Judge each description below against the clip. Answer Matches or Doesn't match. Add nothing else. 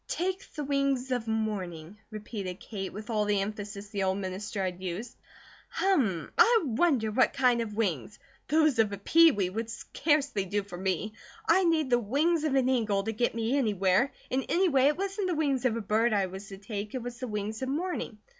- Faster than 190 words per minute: Matches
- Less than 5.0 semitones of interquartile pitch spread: Doesn't match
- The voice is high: Matches